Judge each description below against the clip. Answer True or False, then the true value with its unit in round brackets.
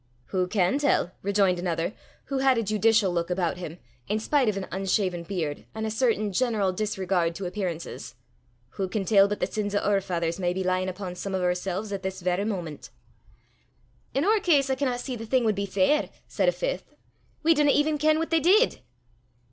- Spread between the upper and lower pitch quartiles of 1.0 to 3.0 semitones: False (5.1 semitones)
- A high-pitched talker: True (200 Hz)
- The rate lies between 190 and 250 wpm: True (205 wpm)